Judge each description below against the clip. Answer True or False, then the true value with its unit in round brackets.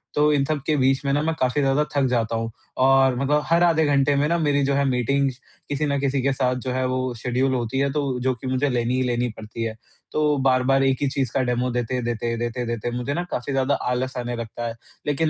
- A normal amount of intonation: False (2.3 semitones)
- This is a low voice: True (130 Hz)